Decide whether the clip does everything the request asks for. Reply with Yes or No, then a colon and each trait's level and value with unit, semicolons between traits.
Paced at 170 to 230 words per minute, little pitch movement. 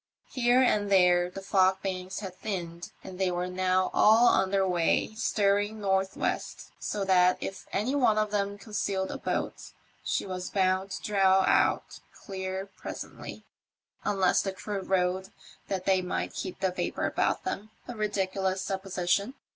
No: average, 160 wpm; narrow, 1.5 semitones